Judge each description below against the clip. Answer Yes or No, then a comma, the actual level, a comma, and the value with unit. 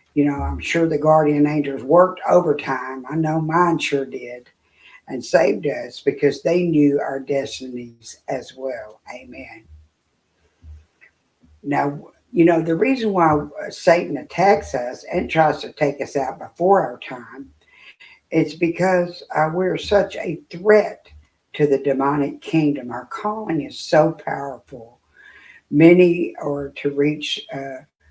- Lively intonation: No, average, 4.2 semitones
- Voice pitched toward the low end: No, medium, 145 Hz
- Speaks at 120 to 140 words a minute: Yes, slow, 135 wpm